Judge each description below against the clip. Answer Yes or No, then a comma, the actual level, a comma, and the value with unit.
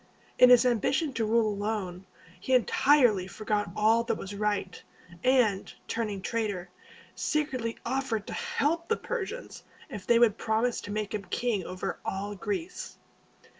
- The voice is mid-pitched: No, high, 225 Hz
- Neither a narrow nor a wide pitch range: Yes, average, 3.9 semitones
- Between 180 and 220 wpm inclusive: No, average, 145 wpm